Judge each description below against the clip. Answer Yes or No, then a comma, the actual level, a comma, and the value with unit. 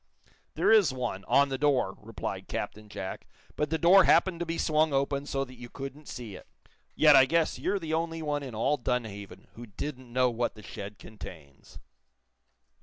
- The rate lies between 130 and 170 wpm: No, average, 185 wpm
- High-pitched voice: No, low, 135 Hz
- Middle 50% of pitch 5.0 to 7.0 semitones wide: Yes, wide, 5.6 semitones